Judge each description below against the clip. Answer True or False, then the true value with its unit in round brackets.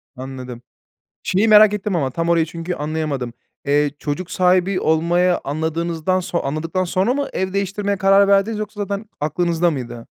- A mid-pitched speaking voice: True (175 Hz)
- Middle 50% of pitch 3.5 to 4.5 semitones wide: True (4.2 semitones)